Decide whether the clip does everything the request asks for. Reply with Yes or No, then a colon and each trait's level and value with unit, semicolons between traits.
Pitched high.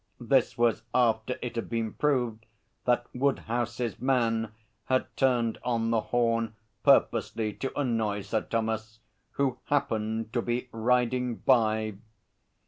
No: low, 115 Hz